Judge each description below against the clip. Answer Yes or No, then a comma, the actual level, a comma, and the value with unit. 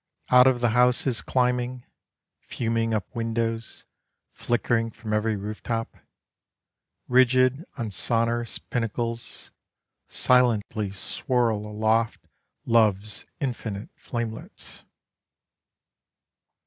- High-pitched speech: No, low, 115 Hz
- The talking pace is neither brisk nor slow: No, slow, 85 wpm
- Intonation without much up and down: Yes, narrow, 2.0 semitones